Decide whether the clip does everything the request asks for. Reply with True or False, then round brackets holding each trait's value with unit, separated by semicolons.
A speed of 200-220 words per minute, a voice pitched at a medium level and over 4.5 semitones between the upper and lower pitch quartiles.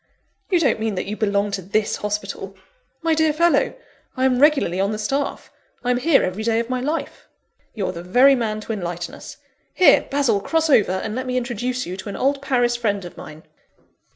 False (205 wpm; 230 Hz; 5.2 semitones)